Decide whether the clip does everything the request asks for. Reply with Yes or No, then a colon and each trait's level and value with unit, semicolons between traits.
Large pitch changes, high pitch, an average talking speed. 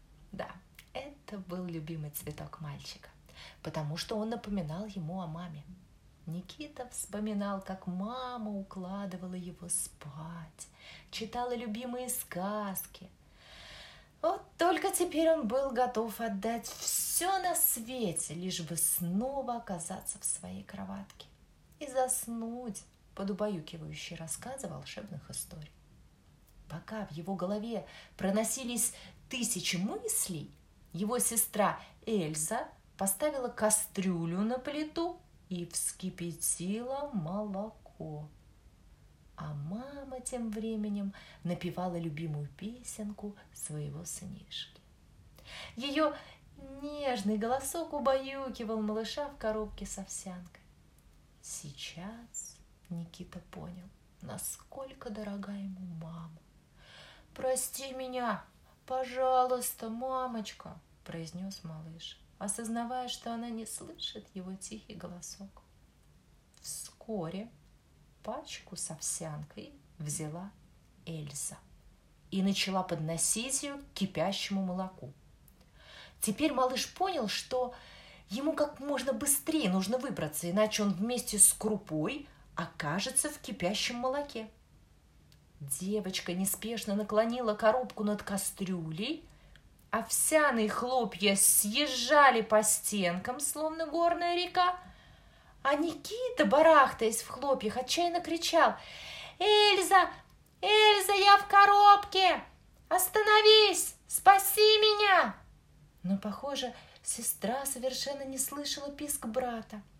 No: wide, 6.7 semitones; high, 215 Hz; slow, 95 wpm